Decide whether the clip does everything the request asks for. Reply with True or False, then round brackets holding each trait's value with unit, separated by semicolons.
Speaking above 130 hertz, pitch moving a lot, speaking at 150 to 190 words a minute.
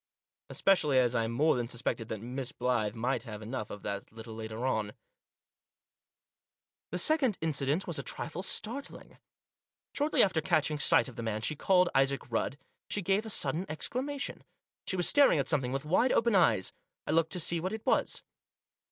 True (140 Hz; 7.9 semitones; 180 wpm)